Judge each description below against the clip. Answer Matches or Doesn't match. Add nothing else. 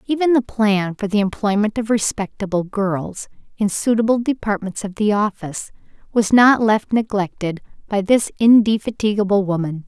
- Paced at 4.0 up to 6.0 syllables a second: Matches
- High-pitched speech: Matches